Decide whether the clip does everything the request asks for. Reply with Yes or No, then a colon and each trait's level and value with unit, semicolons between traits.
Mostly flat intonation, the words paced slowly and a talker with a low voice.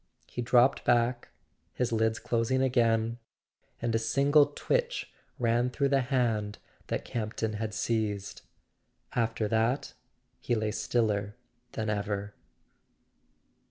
Yes: narrow, 2.3 semitones; slow, 115 wpm; low, 115 Hz